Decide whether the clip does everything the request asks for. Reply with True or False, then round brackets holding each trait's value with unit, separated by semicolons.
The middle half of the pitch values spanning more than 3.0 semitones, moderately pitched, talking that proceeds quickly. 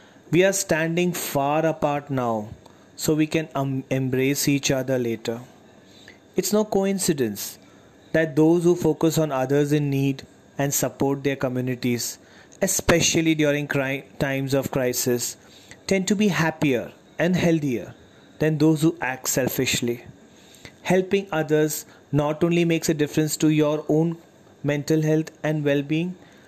False (3.6 semitones; 150 Hz; 140 wpm)